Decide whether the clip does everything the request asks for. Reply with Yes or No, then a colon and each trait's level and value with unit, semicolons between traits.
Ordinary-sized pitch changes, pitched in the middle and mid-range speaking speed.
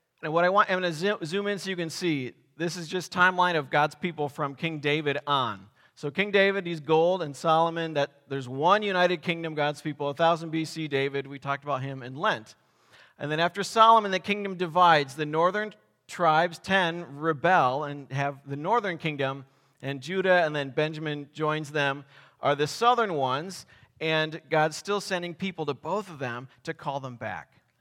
Yes: average, 4.1 semitones; medium, 155 Hz; average, 190 wpm